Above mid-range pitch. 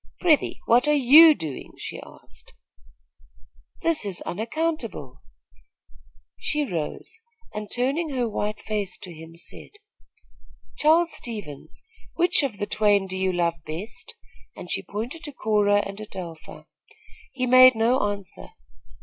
Yes: high, 215 Hz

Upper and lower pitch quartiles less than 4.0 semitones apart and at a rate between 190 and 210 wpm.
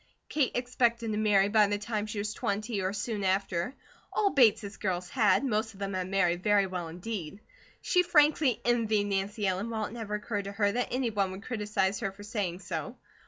Yes: average, 2.9 semitones; fast, 205 wpm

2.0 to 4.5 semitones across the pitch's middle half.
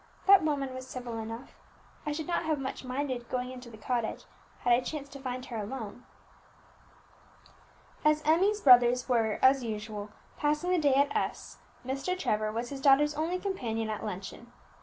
Yes: average, 4.2 semitones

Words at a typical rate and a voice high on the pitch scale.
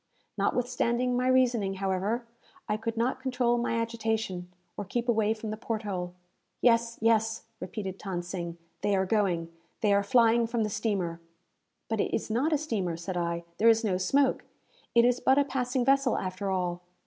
Yes: average, 180 wpm; high, 220 Hz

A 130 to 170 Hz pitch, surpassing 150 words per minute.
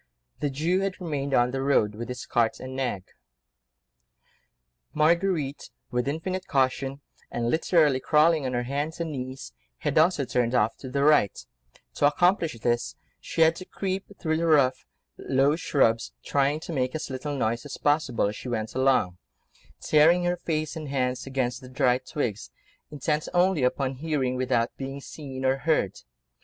Yes: low, 135 Hz; average, 165 wpm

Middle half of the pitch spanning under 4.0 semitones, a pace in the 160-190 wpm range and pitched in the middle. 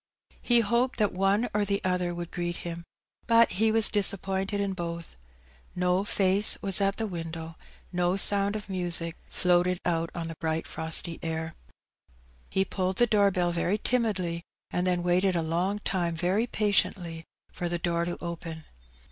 Yes: average, 2.8 semitones; average, 165 wpm; medium, 180 Hz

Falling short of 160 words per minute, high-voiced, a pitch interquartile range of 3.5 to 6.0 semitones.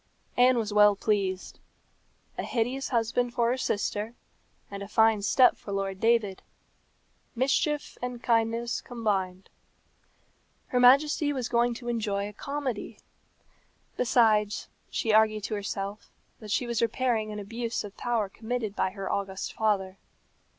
No: slow, 135 wpm; high, 225 Hz; average, 3.0 semitones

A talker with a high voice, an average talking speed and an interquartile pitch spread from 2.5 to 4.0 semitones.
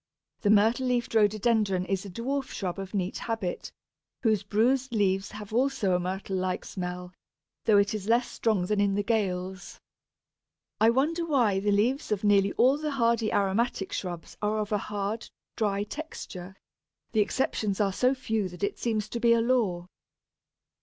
Yes: high, 210 Hz; average, 170 wpm; average, 3.3 semitones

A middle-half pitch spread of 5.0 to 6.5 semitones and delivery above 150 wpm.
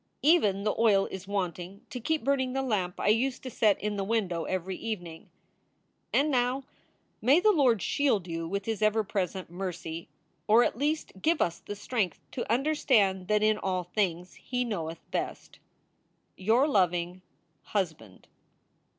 Yes: wide, 5.4 semitones; average, 160 wpm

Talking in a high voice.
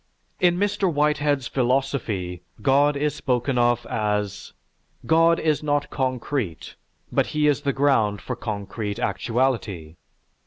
No: low, 130 Hz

